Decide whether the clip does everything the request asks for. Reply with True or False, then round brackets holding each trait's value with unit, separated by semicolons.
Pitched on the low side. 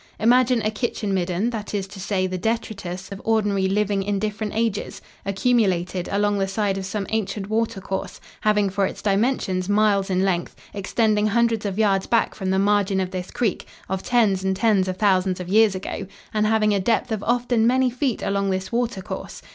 False (205 Hz)